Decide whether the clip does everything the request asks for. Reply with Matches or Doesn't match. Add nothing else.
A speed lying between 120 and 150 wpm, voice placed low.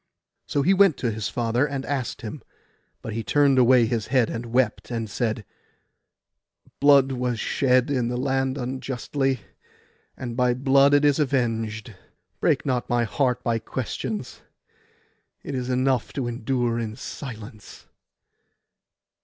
Matches